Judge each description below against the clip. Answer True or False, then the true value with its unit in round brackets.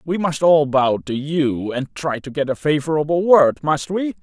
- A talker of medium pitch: True (150 Hz)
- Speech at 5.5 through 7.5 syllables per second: False (4.4 syllables/s)